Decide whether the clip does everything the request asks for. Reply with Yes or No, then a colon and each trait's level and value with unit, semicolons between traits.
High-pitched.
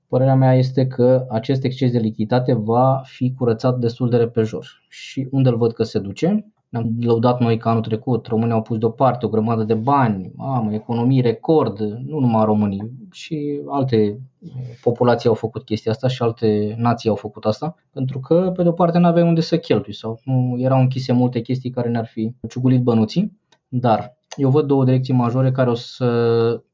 No: low, 125 Hz